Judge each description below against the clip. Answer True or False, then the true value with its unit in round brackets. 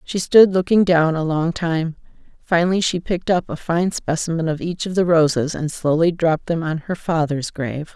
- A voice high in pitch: False (165 Hz)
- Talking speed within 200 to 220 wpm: True (205 wpm)